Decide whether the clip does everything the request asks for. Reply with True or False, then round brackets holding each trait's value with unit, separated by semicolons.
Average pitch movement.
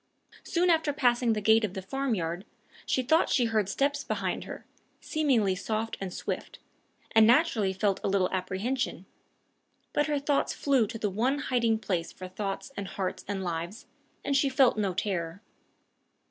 False (5.9 semitones)